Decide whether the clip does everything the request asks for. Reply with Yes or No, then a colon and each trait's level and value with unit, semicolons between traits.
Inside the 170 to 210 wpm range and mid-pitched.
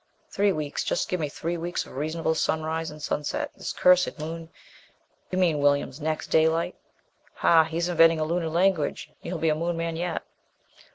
Yes: average, 175 wpm; medium, 165 Hz